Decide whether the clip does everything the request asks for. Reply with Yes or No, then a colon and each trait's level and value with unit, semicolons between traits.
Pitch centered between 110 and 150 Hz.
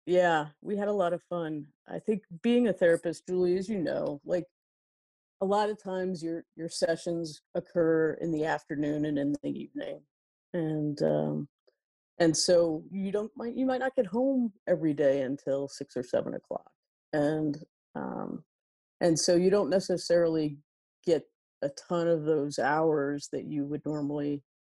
No: medium, 165 Hz